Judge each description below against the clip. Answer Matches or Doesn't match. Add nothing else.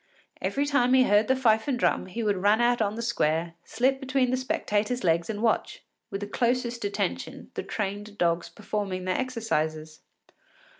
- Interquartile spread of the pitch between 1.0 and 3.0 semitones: Doesn't match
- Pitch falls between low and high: Doesn't match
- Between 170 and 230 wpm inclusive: Matches